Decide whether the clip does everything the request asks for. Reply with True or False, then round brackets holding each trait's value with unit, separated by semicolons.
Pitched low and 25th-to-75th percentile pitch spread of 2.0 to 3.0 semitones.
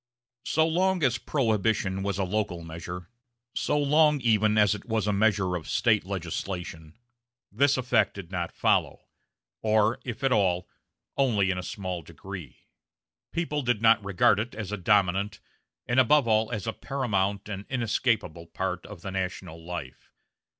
False (105 Hz; 4.3 semitones)